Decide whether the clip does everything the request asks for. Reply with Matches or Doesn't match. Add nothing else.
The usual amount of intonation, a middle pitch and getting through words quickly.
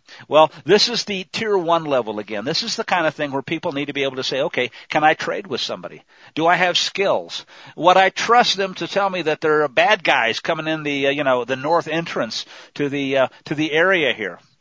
Matches